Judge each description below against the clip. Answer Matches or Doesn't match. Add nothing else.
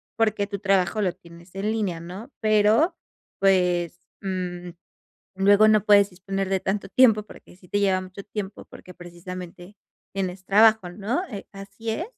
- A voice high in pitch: Matches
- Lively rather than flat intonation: Doesn't match